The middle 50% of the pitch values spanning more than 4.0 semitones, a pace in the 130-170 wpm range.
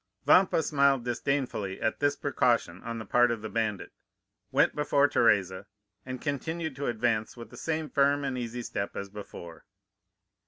Yes: average, 4.6 semitones; average, 160 wpm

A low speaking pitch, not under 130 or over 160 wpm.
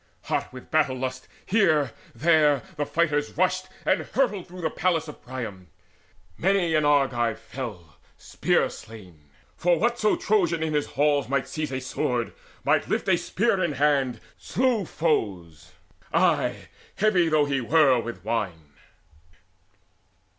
No: medium, 145 Hz; average, 140 wpm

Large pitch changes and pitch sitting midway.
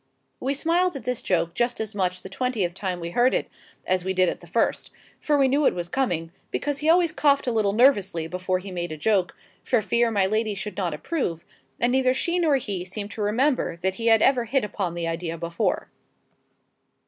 No: wide, 6.3 semitones; high, 210 Hz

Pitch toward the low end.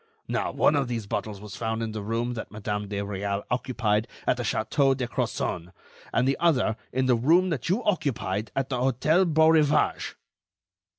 Yes: low, 120 Hz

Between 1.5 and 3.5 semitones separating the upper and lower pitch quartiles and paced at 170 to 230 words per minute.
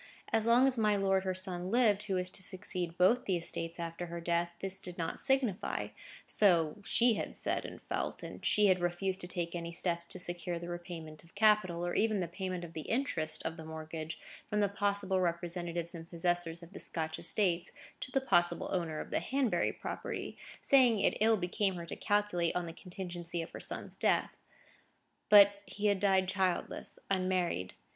Yes: average, 2.9 semitones; average, 195 wpm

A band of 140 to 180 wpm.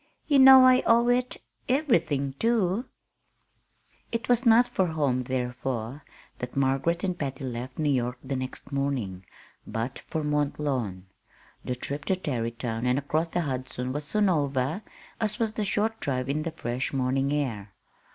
Yes: average, 160 wpm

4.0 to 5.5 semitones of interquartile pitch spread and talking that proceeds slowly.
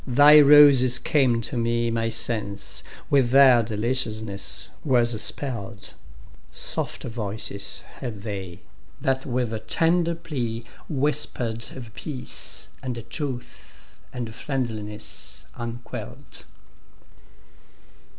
No: average, 3.4 semitones; slow, 80 wpm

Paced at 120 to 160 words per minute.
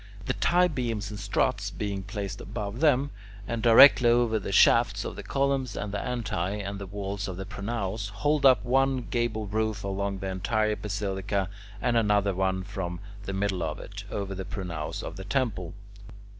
No: average, 170 wpm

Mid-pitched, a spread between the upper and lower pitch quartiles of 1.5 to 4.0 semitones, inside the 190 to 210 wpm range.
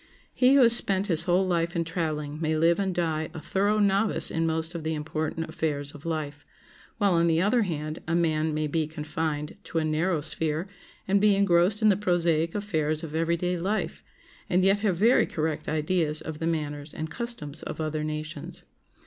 Yes: medium, 165 Hz; average, 3.3 semitones; average, 200 wpm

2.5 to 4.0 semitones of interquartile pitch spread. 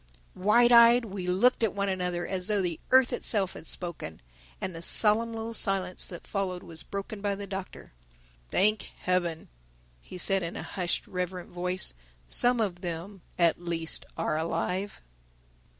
Yes: average, 3.0 semitones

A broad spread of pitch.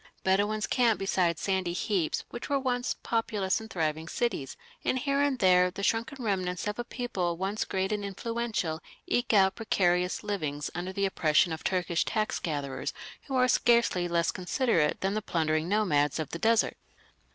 No: average, 4.6 semitones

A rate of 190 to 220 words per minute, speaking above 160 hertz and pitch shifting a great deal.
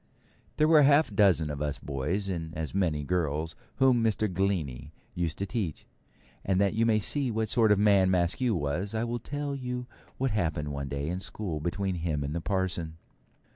No: average, 195 wpm; very low, 95 Hz; wide, 5.8 semitones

